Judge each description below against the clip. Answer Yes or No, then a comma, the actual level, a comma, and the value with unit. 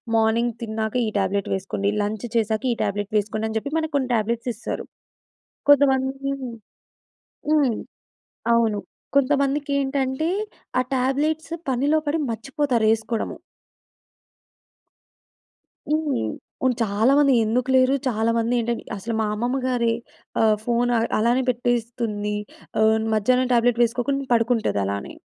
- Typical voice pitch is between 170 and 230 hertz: No, high, 240 Hz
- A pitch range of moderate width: Yes, average, 3.6 semitones